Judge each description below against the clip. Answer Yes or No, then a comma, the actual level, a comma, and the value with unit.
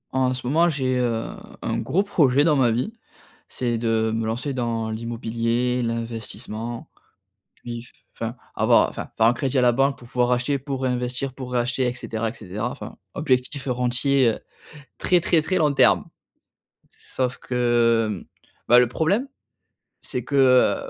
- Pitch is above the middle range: No, low, 125 Hz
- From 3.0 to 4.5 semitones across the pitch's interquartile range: No, narrow, 2.5 semitones